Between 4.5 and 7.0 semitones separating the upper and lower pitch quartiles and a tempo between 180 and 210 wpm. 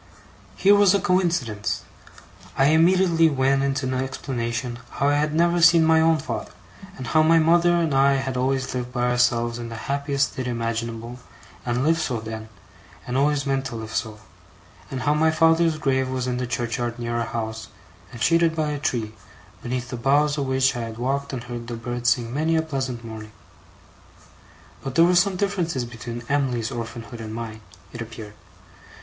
Yes: average, 4.8 semitones; average, 185 wpm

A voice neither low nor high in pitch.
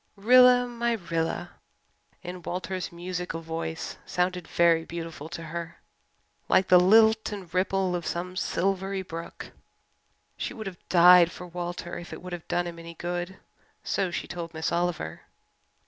Yes: medium, 175 Hz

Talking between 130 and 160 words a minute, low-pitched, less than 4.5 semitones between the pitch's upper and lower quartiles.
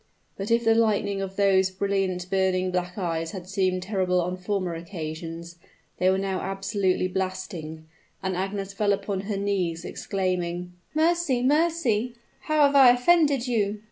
No: average, 150 wpm; high, 195 Hz; average, 2.8 semitones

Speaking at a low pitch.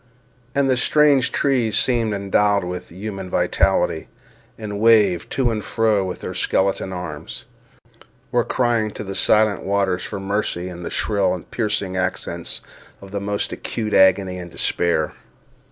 Yes: low, 100 Hz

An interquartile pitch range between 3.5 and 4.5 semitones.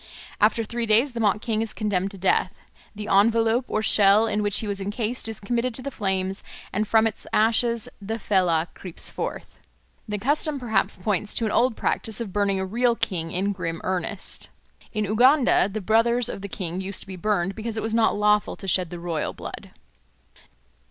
No: average, 2.8 semitones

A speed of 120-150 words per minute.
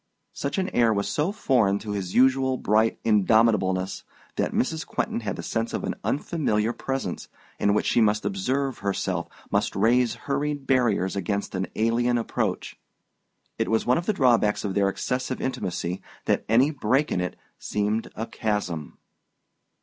No: average, 160 wpm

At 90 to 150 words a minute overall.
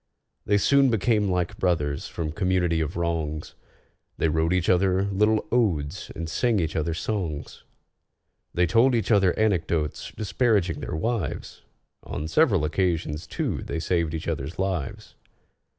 Yes: average, 140 wpm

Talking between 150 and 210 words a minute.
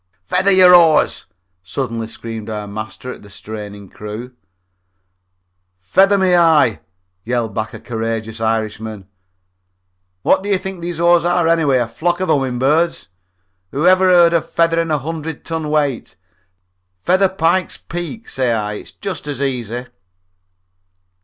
No: average, 140 wpm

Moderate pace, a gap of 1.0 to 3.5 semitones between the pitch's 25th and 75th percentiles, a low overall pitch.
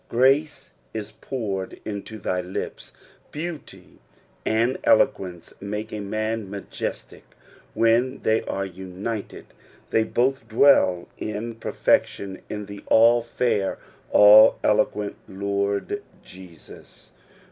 No: slow, 105 wpm; average, 2.9 semitones; low, 105 Hz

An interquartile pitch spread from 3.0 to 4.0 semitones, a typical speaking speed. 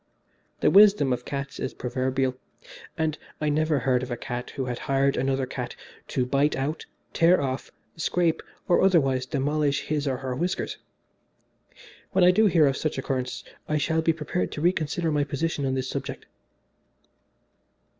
Yes: average, 3.5 semitones; average, 170 wpm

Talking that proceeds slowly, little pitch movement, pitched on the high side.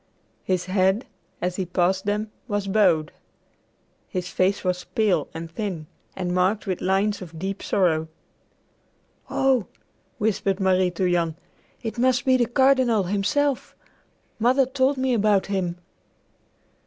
No: slow, 130 wpm; average, 3.6 semitones; high, 195 Hz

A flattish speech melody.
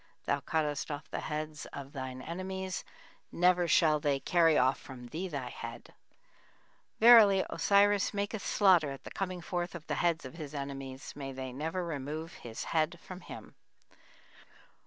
No: average, 4.7 semitones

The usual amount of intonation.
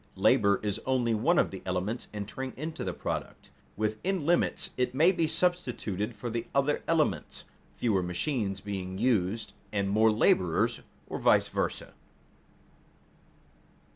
No: wide, 5.7 semitones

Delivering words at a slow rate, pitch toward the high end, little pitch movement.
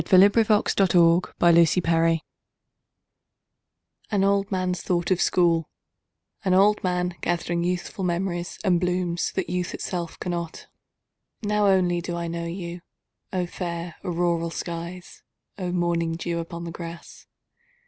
No: slow, 130 wpm; medium, 175 Hz; narrow, 1.4 semitones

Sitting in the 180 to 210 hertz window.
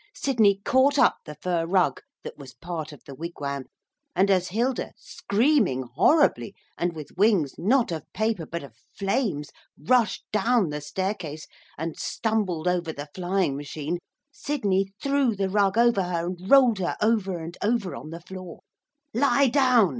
Yes: high, 190 Hz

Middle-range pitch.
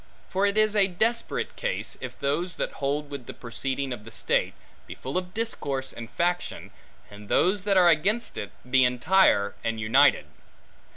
Yes: medium, 145 Hz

